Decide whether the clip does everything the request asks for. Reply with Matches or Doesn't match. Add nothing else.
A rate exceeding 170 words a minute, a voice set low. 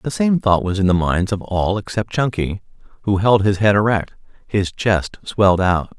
Matches